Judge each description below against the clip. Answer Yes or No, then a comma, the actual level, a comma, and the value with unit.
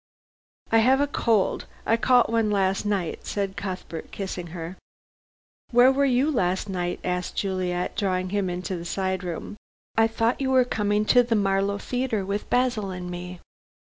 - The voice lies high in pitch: Yes, high, 200 Hz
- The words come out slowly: No, average, 170 wpm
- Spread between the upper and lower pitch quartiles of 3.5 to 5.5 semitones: Yes, average, 3.9 semitones